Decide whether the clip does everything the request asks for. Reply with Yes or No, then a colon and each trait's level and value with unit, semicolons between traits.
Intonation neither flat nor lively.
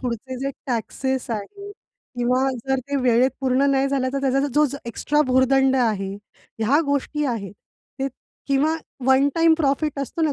No: narrow, 2.0 semitones